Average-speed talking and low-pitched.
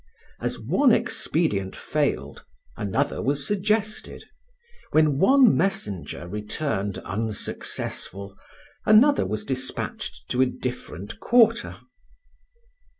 No: slow, 90 wpm; low, 130 Hz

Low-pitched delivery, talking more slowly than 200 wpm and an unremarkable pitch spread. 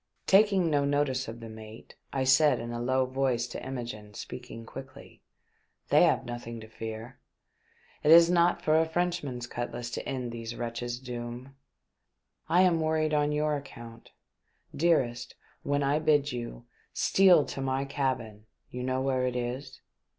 Yes: low, 130 Hz; average, 165 wpm; average, 3.8 semitones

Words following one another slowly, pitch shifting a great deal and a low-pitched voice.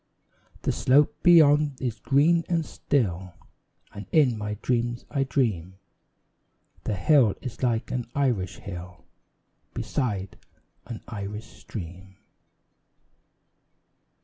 Yes: slow, 100 wpm; wide, 6.2 semitones; low, 120 Hz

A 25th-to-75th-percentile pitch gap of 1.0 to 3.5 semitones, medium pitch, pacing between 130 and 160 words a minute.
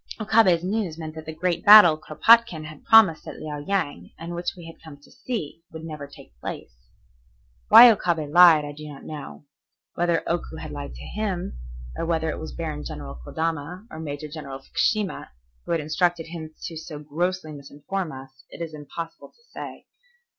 No: average, 2.9 semitones; medium, 160 Hz; average, 180 wpm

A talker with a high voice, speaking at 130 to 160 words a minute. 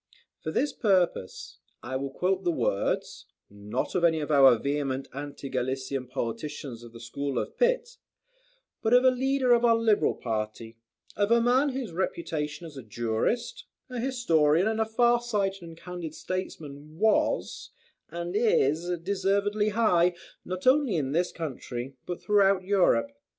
No: medium, 175 Hz; average, 155 wpm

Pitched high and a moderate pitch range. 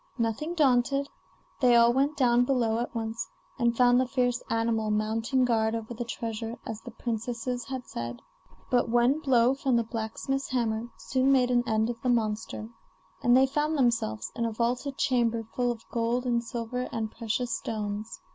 No: high, 240 Hz; narrow, 1.9 semitones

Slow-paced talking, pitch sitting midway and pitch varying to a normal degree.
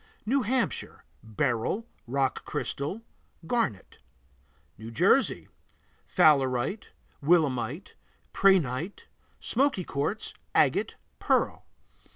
No: slow, 75 wpm; medium, 150 Hz; wide, 8.5 semitones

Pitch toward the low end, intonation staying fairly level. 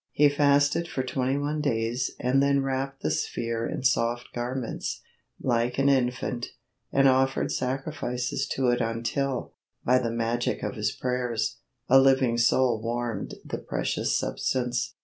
Yes: low, 125 Hz; narrow, 2.3 semitones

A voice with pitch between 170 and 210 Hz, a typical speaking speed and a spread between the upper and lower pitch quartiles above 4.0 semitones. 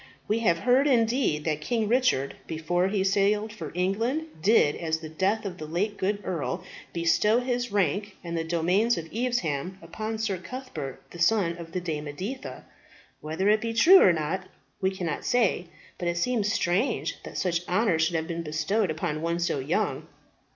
Yes: medium, 185 Hz; average, 180 wpm; average, 5.0 semitones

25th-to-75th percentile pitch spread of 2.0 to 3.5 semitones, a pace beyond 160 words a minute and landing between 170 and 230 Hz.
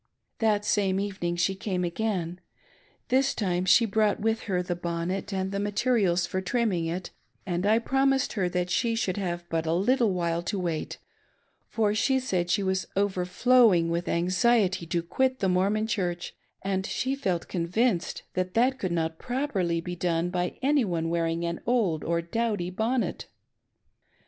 No: average, 4.2 semitones; average, 170 wpm; high, 190 Hz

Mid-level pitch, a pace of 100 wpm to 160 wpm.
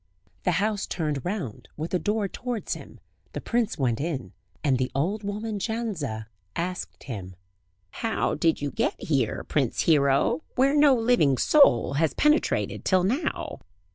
Yes: medium, 175 Hz; average, 150 wpm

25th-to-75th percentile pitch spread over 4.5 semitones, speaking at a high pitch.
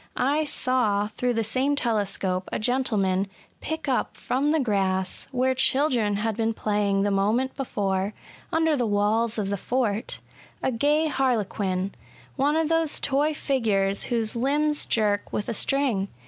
Yes: average, 5.0 semitones; high, 230 Hz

